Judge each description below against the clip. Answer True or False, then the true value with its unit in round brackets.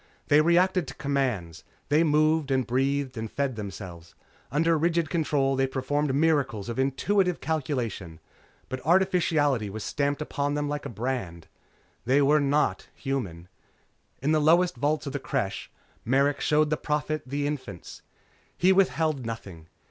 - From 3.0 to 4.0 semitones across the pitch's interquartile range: True (3.5 semitones)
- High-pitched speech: False (140 Hz)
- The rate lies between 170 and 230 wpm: False (150 wpm)